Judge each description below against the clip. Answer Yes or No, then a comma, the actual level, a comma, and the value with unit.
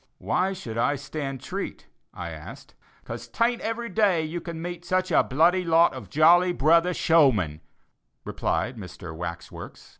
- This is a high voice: No, medium, 165 Hz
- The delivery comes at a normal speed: Yes, average, 155 wpm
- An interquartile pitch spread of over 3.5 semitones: Yes, average, 5.2 semitones